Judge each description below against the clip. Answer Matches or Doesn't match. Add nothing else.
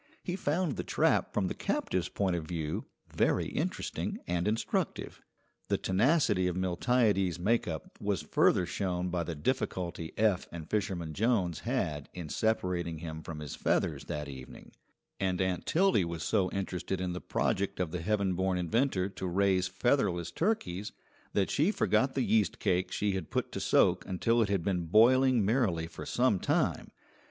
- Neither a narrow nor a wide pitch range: Matches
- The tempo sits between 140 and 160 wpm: Doesn't match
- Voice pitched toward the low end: Matches